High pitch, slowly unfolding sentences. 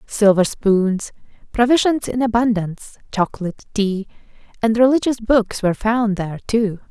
Yes: high, 220 Hz; slow, 120 wpm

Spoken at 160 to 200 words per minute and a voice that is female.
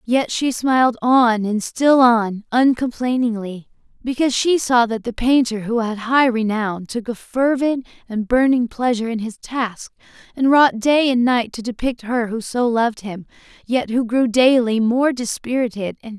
Yes: average, 175 wpm; female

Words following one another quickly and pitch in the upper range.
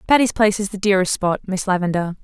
Yes: fast, 215 wpm; high, 195 Hz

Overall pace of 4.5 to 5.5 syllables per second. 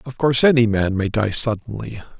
No: 5.8 syllables/s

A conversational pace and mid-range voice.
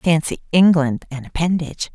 No: slow, 125 wpm; medium, 160 Hz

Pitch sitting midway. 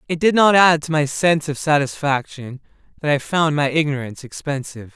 Yes: medium, 150 Hz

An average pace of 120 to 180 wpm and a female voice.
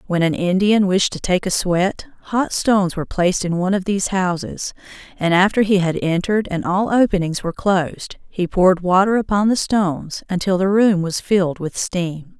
No: average, 195 wpm; female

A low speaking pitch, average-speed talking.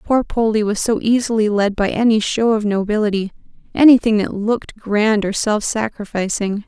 No: high, 215 Hz; average, 155 wpm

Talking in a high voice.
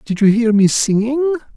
Yes: high, 240 Hz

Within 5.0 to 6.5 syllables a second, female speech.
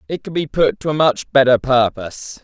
No: 5.3 syllables/s; male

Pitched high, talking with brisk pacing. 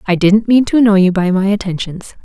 Yes: high, 200 Hz; fast, 240 wpm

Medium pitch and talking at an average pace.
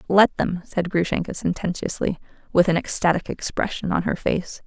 Yes: medium, 180 Hz; average, 155 wpm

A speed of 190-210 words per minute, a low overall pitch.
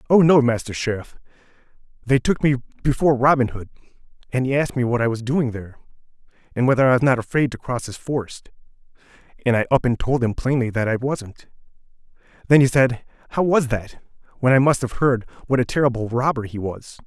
Yes: average, 195 wpm; low, 125 Hz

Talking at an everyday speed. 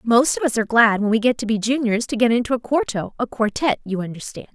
No: fast, 250 wpm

